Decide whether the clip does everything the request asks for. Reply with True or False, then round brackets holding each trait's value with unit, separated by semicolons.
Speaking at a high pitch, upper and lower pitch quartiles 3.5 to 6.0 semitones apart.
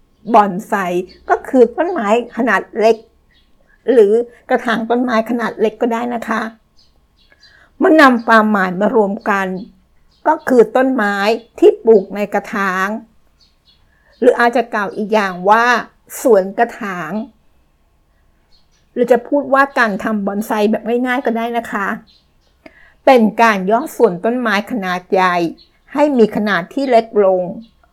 False (220 Hz; 3.1 semitones)